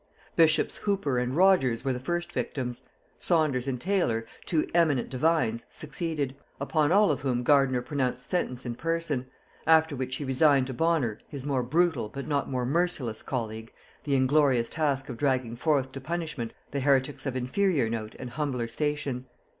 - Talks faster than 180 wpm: No, average, 165 wpm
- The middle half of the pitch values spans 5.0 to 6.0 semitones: No, average, 3.9 semitones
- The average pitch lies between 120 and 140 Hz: Yes, low, 135 Hz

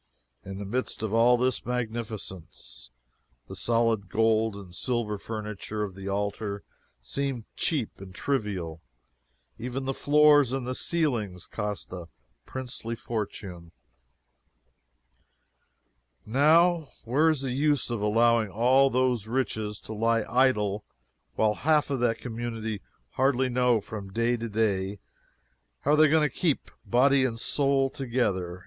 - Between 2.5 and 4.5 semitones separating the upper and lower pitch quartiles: Yes, average, 4.1 semitones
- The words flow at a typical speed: No, slow, 130 wpm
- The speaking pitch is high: No, low, 115 Hz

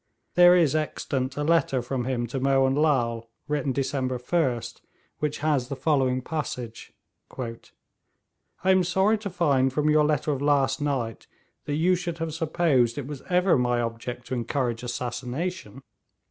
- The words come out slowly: No, average, 155 wpm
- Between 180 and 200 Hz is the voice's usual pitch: No, low, 135 Hz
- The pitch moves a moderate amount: Yes, average, 4.0 semitones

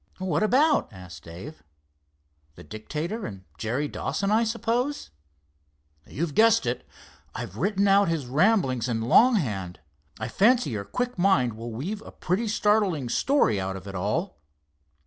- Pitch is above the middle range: No, medium, 150 Hz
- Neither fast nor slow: Yes, average, 145 wpm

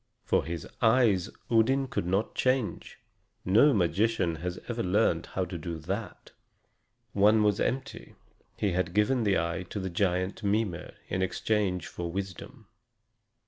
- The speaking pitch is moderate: No, low, 100 Hz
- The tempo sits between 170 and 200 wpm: No, average, 140 wpm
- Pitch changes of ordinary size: Yes, average, 3.9 semitones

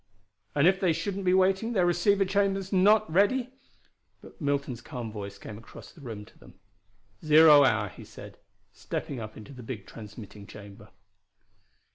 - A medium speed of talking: Yes, average, 165 wpm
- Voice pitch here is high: No, medium, 150 Hz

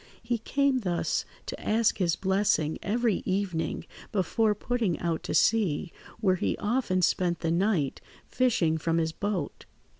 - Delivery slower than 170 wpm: Yes, average, 145 wpm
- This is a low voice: No, high, 195 Hz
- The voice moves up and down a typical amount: Yes, average, 4.7 semitones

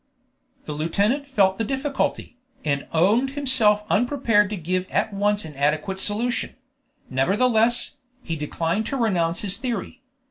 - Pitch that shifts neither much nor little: No, wide, 6.1 semitones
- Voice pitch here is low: No, high, 205 Hz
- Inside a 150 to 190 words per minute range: No, slow, 135 wpm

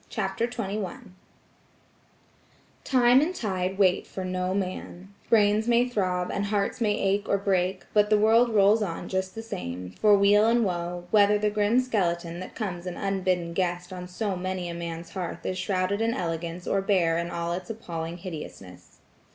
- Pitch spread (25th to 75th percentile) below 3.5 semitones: Yes, average, 3.0 semitones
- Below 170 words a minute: No, average, 175 wpm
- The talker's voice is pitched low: No, high, 190 Hz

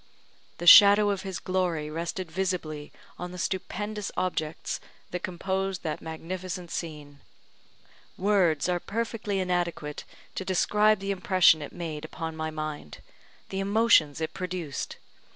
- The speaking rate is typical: No, slow, 130 wpm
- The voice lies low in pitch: No, medium, 180 Hz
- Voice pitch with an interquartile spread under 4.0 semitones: Yes, average, 3.3 semitones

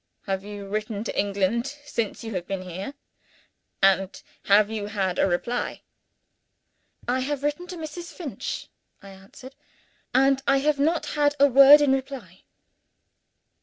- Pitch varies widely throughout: Yes, wide, 6.2 semitones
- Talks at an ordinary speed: Yes, average, 145 wpm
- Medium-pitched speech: No, high, 235 Hz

